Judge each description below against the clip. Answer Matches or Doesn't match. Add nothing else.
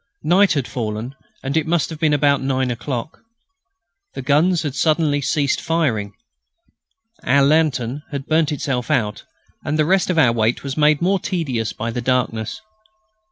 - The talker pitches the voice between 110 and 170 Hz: Matches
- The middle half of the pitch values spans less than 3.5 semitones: Doesn't match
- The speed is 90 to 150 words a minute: Doesn't match